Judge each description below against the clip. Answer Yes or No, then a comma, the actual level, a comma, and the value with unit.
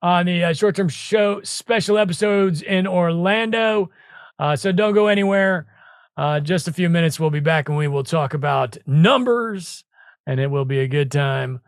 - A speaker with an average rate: Yes, average, 180 wpm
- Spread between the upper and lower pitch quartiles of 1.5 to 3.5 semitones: No, average, 5.3 semitones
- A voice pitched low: No, medium, 175 Hz